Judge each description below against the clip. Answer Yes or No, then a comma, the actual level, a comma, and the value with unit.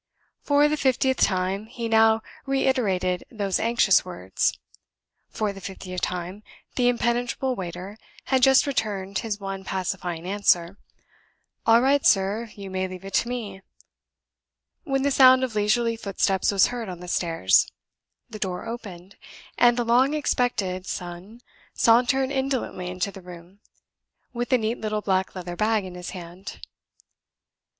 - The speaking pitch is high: Yes, high, 210 Hz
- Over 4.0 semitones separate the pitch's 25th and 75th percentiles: Yes, average, 4.6 semitones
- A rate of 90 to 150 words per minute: Yes, average, 145 wpm